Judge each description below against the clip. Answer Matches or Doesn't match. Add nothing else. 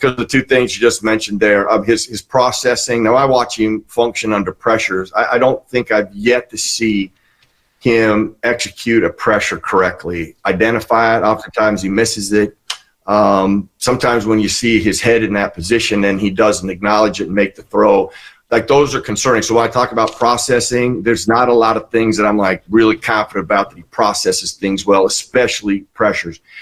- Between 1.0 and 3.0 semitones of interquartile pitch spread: Matches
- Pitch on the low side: Matches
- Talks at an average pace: Matches